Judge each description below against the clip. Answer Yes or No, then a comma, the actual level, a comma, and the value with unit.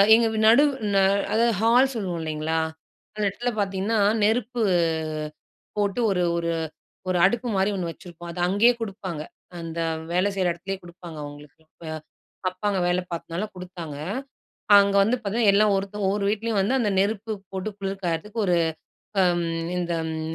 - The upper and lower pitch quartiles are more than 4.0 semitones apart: No, average, 3.7 semitones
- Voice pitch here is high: Yes, high, 195 Hz